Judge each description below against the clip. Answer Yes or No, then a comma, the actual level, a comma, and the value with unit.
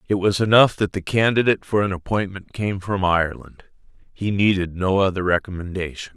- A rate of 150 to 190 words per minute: Yes, average, 165 wpm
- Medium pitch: No, very low, 95 Hz